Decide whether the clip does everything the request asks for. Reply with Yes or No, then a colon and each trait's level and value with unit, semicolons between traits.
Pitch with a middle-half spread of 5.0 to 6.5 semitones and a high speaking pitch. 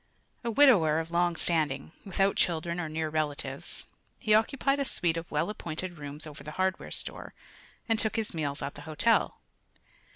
No: average, 5.3 semitones; medium, 170 Hz